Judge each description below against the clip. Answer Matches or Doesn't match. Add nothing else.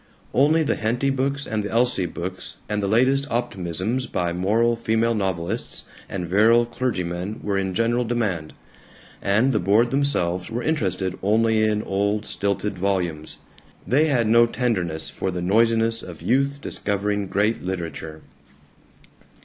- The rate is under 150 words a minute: Matches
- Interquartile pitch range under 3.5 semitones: Doesn't match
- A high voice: Doesn't match